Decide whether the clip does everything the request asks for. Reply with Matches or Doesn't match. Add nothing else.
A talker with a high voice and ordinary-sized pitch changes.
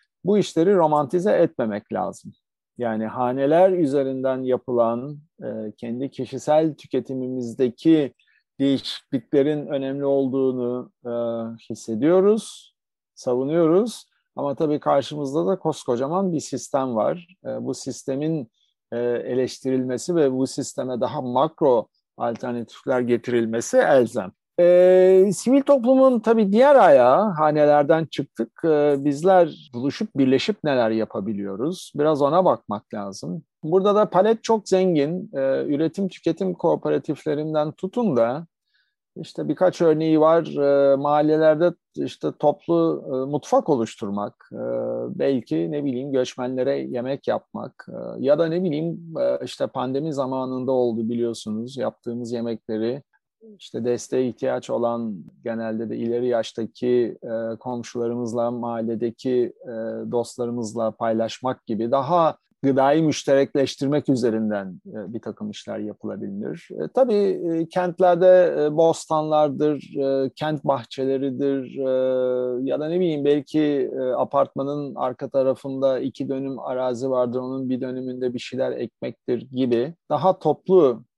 Doesn't match